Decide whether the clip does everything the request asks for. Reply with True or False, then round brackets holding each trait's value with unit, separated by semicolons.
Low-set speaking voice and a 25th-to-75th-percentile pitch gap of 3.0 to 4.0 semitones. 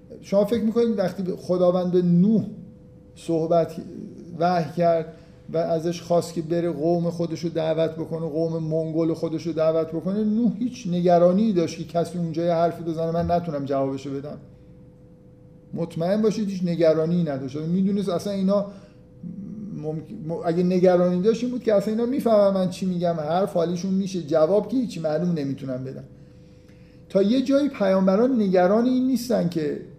False (175 Hz; 3.3 semitones)